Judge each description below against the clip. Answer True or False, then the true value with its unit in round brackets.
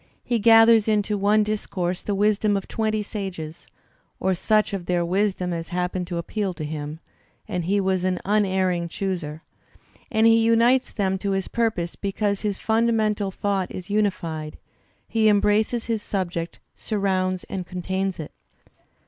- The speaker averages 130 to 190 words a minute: True (150 wpm)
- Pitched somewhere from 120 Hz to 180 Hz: False (195 Hz)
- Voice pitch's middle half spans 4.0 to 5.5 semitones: False (3.0 semitones)